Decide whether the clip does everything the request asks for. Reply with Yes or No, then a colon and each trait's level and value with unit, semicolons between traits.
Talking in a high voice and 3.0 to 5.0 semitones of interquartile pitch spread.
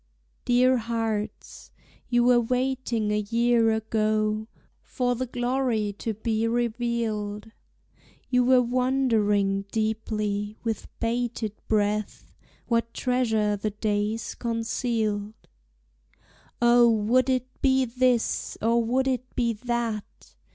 No: high, 230 Hz; narrow, 2.4 semitones